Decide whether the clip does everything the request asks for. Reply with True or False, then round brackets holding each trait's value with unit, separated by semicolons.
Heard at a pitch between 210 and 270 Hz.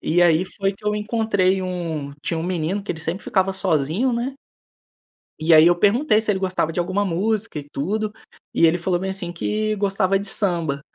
False (190 Hz)